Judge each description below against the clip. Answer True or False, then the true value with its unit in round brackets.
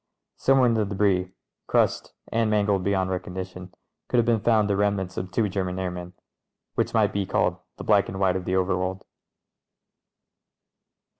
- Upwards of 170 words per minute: False (165 wpm)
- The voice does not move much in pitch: True (2.1 semitones)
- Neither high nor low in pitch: False (95 Hz)